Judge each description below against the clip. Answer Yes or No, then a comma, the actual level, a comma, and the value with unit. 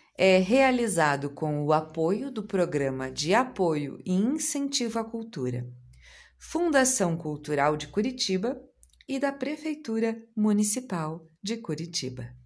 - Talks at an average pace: No, slow, 110 wpm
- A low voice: No, high, 190 Hz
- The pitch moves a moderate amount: No, wide, 8.5 semitones